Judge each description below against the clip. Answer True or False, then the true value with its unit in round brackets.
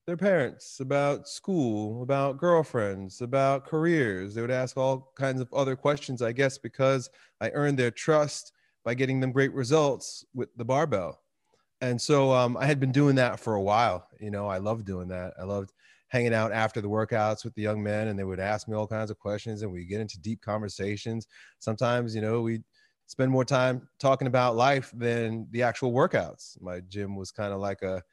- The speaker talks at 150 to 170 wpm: False (205 wpm)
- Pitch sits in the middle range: False (120 Hz)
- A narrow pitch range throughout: False (4.1 semitones)